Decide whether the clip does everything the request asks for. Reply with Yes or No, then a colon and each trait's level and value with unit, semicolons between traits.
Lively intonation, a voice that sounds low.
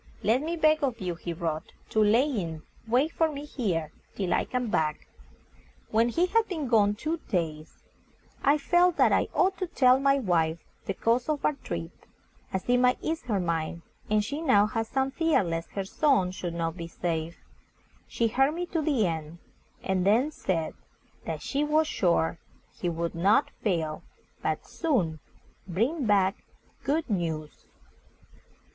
No: wide, 9.0 semitones; high, 215 Hz